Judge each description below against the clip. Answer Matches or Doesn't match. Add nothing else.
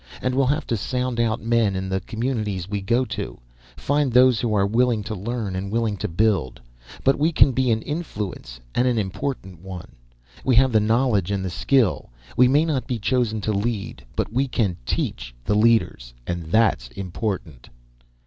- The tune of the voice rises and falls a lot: Doesn't match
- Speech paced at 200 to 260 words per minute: Doesn't match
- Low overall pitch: Matches